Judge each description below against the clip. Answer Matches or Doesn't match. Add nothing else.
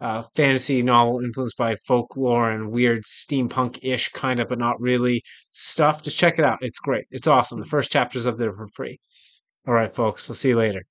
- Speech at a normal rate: Doesn't match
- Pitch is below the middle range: Matches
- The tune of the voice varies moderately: Doesn't match